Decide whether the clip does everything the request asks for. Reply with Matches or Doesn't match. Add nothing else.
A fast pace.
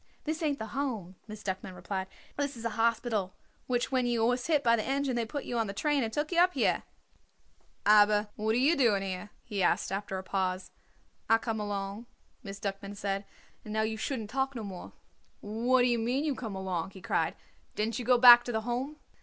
Matches